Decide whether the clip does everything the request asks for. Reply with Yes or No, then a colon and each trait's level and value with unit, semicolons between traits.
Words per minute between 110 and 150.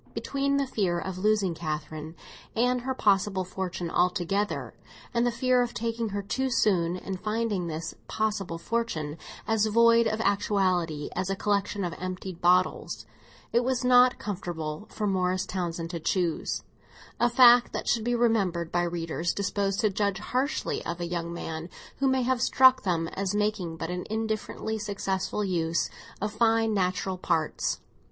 No: average, 160 wpm